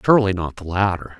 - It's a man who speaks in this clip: Yes, male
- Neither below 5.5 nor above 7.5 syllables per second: Yes, 6.5 syllables/s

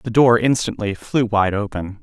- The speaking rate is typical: Yes, average, 180 wpm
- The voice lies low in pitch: Yes, low, 110 Hz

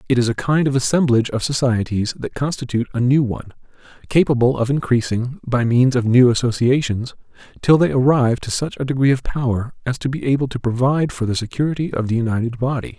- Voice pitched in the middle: No, low, 125 Hz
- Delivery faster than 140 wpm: Yes, average, 200 wpm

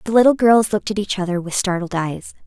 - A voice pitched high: Yes, high, 195 Hz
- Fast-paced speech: Yes, fast, 245 wpm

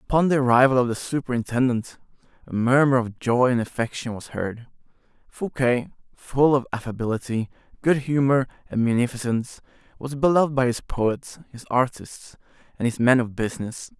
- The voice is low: Yes, low, 125 Hz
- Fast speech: No, average, 145 wpm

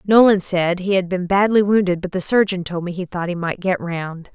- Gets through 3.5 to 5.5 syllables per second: Yes, 5.2 syllables/s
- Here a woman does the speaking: Yes, female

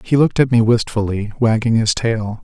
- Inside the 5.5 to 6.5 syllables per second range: No, 5.3 syllables/s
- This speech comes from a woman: No, male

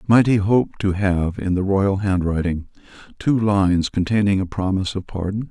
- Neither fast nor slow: Yes, average, 175 wpm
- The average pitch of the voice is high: No, low, 100 Hz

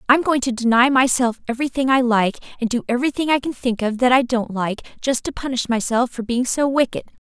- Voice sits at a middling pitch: No, very high, 250 Hz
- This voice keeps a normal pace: No, fast, 225 wpm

